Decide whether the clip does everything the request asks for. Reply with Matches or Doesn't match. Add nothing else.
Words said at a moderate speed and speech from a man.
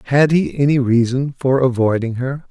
Matches